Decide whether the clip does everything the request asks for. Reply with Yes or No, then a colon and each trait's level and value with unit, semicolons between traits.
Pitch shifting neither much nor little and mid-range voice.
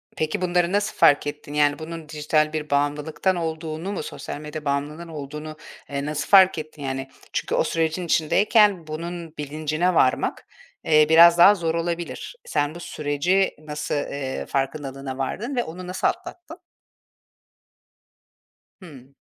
Yes: average, 3.0 semitones; medium, 155 Hz